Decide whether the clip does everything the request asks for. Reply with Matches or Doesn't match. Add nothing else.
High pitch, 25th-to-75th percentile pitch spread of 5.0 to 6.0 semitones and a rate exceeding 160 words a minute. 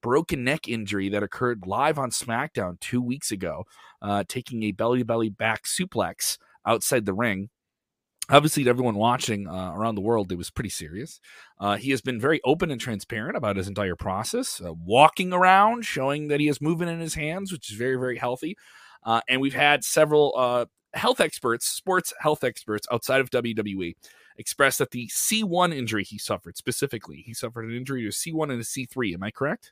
Doesn't match